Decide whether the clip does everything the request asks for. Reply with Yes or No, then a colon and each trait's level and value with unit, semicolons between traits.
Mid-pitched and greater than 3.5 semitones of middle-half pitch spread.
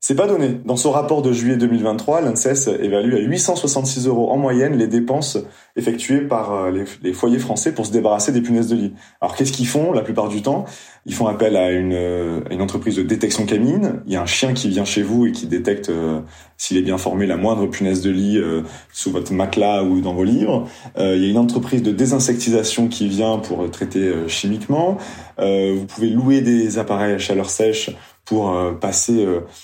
No: low, 110 Hz; average, 4.2 semitones